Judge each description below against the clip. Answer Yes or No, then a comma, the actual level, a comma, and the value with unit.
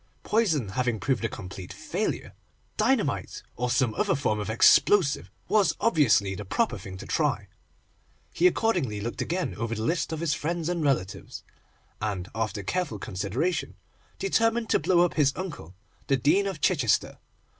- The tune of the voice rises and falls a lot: Yes, wide, 8.6 semitones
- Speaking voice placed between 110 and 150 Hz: Yes, low, 135 Hz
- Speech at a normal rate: Yes, average, 155 wpm